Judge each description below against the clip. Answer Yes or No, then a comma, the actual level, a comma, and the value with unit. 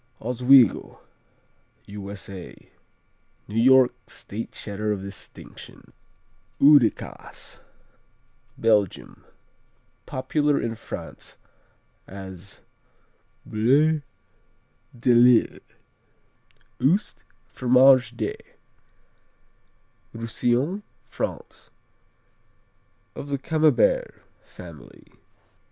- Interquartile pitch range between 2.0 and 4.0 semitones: No, average, 4.5 semitones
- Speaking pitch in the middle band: No, low, 120 Hz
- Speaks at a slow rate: Yes, slow, 65 wpm